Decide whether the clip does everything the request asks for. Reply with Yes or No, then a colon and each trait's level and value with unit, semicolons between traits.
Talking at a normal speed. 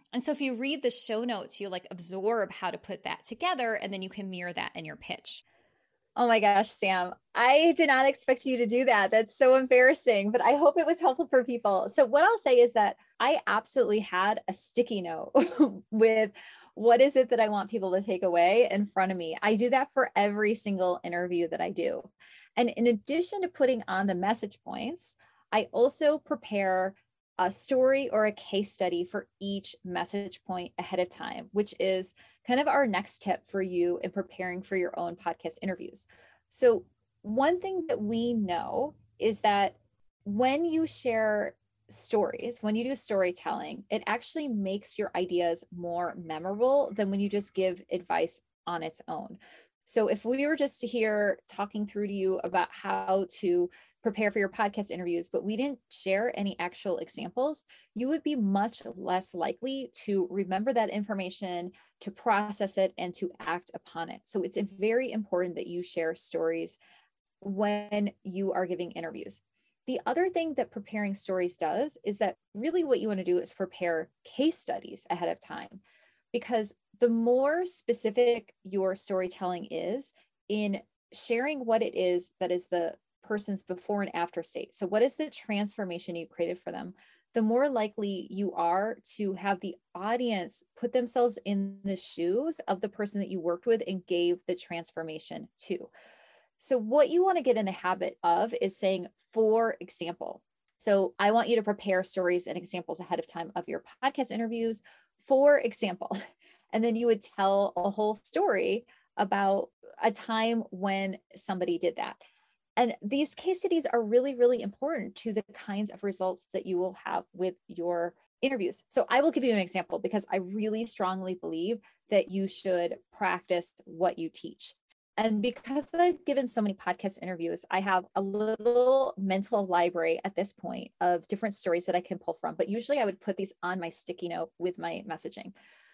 Yes: average, 185 wpm